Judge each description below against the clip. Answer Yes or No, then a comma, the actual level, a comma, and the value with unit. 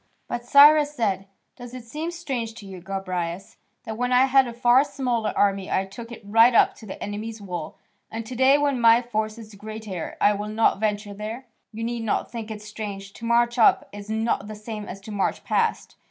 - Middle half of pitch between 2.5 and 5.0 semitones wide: Yes, average, 2.8 semitones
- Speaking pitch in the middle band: No, high, 220 Hz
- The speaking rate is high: Yes, fast, 210 wpm